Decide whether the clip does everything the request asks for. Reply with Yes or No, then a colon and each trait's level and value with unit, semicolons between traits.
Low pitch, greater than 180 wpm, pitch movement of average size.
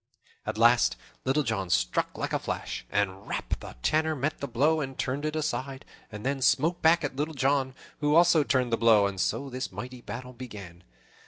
Yes: low, 130 Hz; average, 195 wpm; average, 4.3 semitones